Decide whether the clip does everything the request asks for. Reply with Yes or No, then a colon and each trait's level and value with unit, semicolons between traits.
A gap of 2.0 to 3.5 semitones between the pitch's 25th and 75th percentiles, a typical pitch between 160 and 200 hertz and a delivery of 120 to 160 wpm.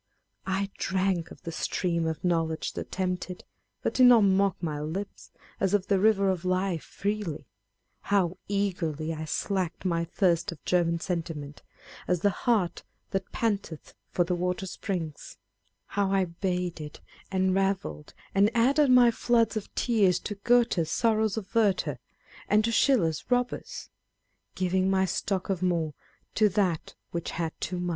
Yes: average, 3.2 semitones; medium, 185 Hz; average, 155 wpm